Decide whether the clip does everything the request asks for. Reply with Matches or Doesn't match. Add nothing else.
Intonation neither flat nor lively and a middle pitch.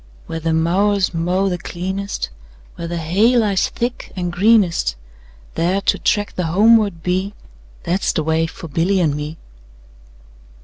Matches